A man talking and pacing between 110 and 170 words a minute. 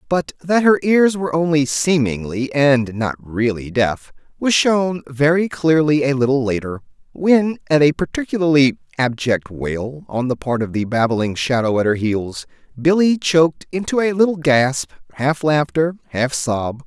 Yes: male; average, 155 wpm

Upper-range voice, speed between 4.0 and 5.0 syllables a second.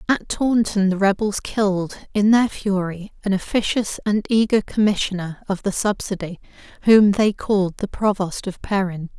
Yes: high, 200 Hz; 4.7 syllables/s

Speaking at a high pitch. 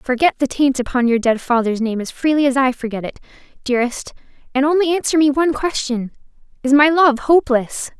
Yes: very high, 265 Hz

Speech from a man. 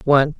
No: female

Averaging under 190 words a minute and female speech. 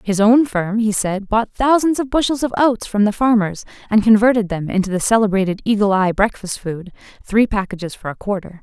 No: average, 200 wpm; female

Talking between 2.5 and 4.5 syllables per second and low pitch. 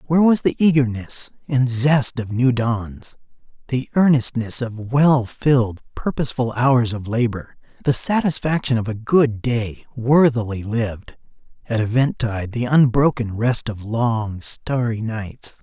Yes: 4.2 syllables/s; low, 120 Hz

